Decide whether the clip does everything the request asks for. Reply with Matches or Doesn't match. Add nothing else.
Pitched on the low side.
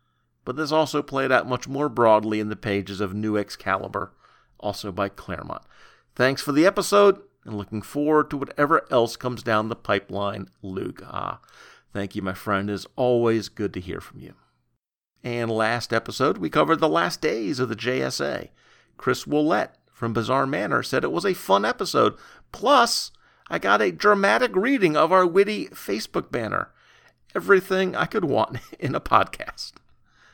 Matches